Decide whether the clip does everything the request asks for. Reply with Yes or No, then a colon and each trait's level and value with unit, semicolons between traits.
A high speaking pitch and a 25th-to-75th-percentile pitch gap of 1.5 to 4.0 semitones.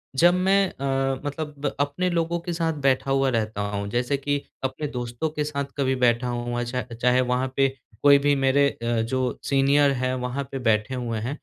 No: low, 135 Hz; average, 2.7 semitones